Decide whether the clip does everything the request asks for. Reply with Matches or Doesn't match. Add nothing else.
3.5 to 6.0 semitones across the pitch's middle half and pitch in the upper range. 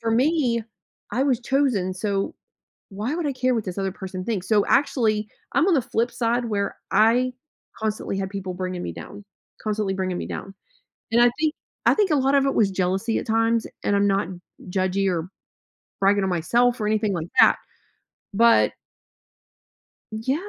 Matches